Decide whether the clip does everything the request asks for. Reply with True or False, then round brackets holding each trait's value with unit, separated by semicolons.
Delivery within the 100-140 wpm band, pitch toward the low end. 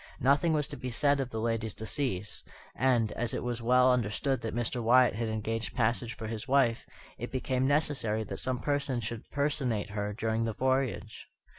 False (185 wpm; 120 Hz)